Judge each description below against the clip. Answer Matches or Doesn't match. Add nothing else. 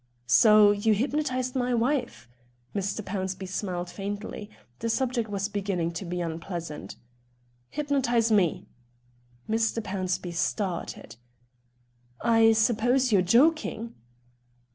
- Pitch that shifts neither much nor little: Matches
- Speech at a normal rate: Doesn't match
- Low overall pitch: Doesn't match